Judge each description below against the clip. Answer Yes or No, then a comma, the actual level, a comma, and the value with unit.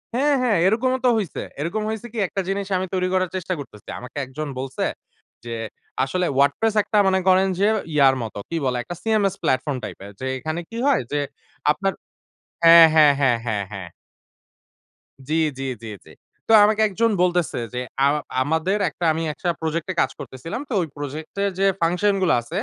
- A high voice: No, medium, 175 Hz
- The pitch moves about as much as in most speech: No, wide, 5.8 semitones